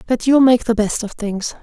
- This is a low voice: No, high, 230 Hz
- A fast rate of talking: Yes, fast, 260 wpm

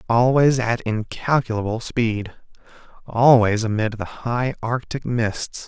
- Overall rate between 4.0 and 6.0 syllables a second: No, 3.8 syllables/s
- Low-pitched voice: Yes, low, 115 Hz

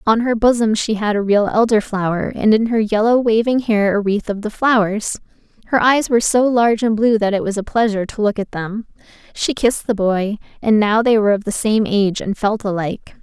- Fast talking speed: Yes, fast, 225 wpm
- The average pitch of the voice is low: No, high, 215 Hz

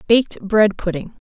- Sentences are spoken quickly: No, average, 140 wpm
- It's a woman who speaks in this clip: Yes, female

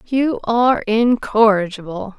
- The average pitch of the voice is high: Yes, high, 220 Hz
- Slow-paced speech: Yes, slow, 80 wpm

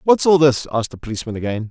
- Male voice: Yes, male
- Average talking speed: No, fast, 245 wpm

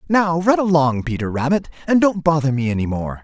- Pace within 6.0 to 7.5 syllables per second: No, 5.5 syllables/s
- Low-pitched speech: No, medium, 155 Hz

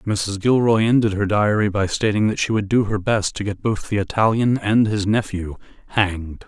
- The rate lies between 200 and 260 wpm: Yes, fast, 205 wpm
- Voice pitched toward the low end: Yes, low, 105 Hz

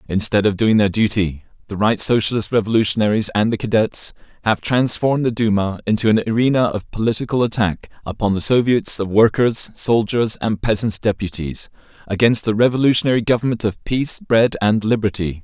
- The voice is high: No, low, 110 Hz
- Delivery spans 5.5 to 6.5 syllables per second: Yes, 5.6 syllables/s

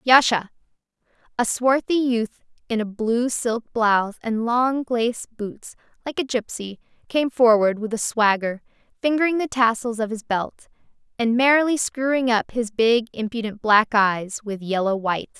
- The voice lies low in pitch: No, high, 230 Hz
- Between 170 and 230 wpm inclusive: No, average, 150 wpm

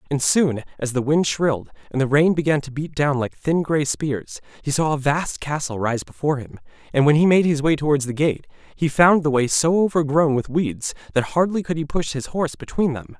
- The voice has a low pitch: No, medium, 150 Hz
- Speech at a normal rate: No, fast, 230 wpm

